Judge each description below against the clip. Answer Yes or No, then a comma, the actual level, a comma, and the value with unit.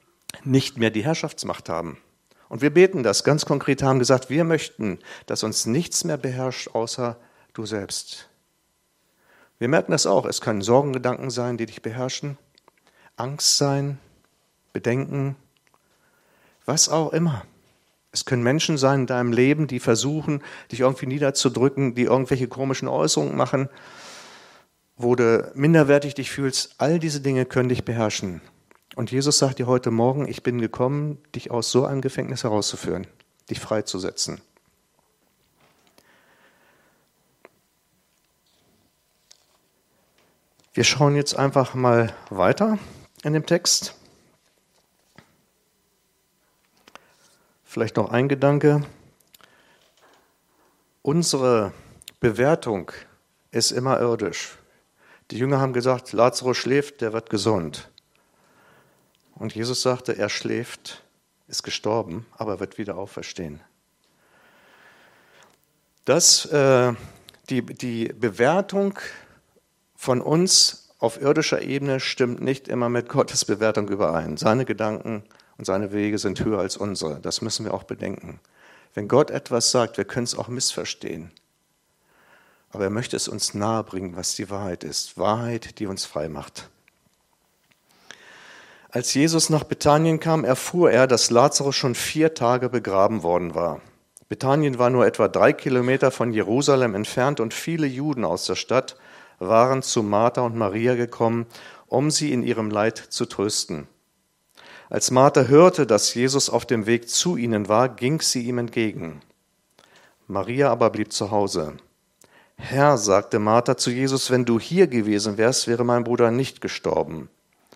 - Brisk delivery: No, average, 130 wpm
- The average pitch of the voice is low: Yes, low, 125 Hz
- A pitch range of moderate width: Yes, average, 3.5 semitones